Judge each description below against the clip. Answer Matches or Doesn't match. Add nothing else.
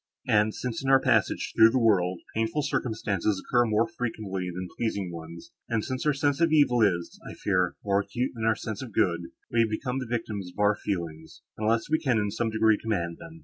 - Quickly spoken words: Matches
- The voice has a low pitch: Matches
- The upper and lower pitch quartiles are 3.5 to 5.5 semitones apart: Matches